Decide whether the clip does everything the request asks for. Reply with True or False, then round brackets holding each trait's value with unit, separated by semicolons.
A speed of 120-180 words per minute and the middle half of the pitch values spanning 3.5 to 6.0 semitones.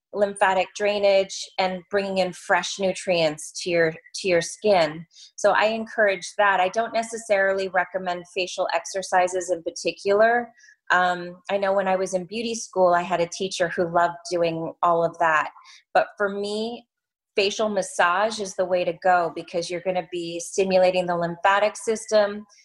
False (165 wpm; 2.6 semitones)